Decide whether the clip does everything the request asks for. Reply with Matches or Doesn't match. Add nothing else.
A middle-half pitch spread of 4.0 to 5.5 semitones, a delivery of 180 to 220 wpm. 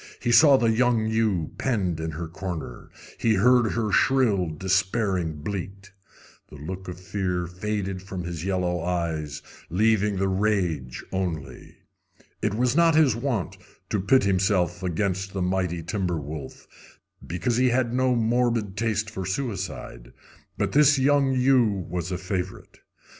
Doesn't match